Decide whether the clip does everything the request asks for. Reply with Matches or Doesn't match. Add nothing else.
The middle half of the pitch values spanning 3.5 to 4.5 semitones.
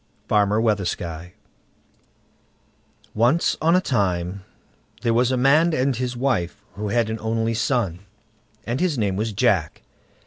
Matches